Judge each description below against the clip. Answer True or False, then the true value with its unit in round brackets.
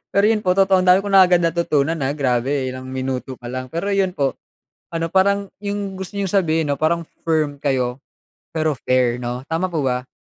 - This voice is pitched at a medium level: True (160 Hz)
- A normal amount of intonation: False (6.2 semitones)